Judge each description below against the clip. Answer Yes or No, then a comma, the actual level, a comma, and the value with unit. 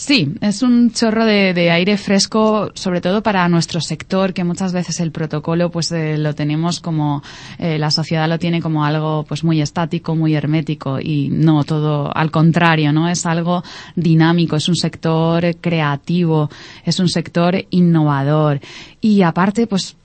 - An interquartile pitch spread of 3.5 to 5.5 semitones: No, narrow, 2.5 semitones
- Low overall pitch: No, medium, 165 Hz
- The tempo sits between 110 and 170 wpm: Yes, average, 165 wpm